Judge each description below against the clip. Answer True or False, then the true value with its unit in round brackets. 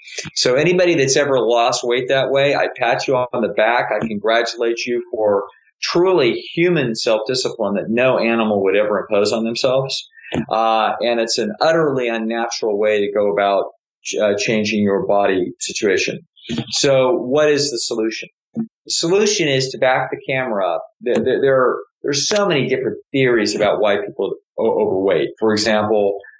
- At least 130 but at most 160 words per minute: False (170 wpm)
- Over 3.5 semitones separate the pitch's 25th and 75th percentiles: True (4.9 semitones)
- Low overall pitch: True (120 Hz)